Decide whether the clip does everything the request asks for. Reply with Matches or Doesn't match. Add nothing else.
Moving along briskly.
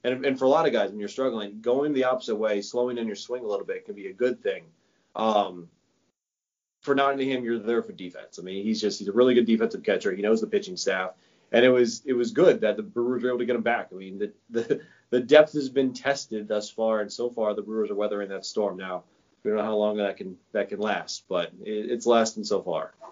Matches